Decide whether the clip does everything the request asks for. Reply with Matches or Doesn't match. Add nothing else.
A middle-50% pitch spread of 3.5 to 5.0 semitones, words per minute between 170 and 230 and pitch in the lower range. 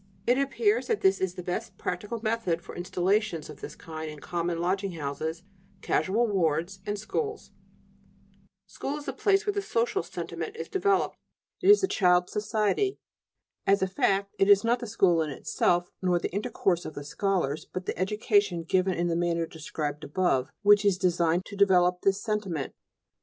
Doesn't match